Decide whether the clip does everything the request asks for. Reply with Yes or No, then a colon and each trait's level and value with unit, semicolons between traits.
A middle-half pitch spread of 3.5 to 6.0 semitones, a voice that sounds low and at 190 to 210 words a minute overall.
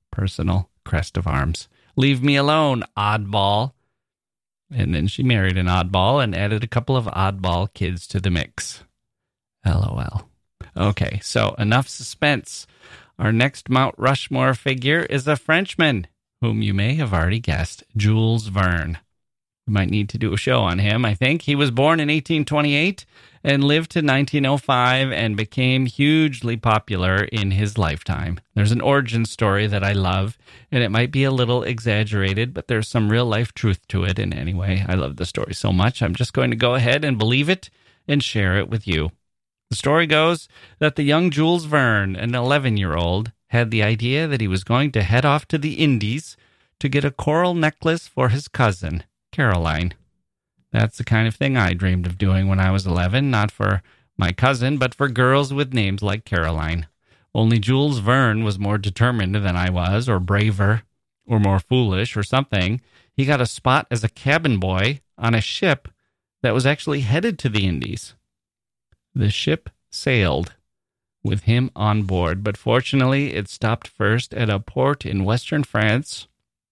No: average, 5.2 semitones; low, 115 Hz; average, 175 wpm